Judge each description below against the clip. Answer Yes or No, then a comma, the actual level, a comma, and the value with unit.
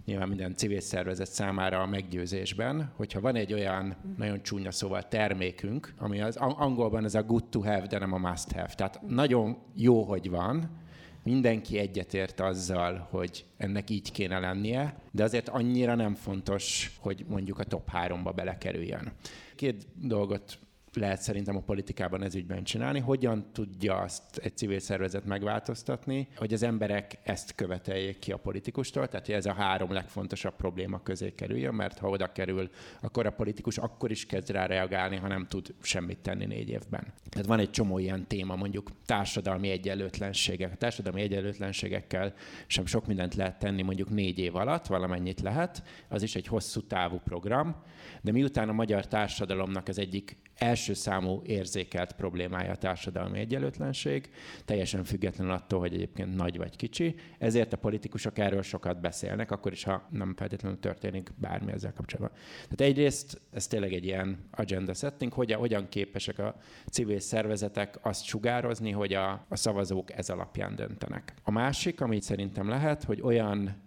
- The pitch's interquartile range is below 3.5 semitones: Yes, average, 2.8 semitones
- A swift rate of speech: Yes, fast, 165 wpm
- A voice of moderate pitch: No, low, 100 Hz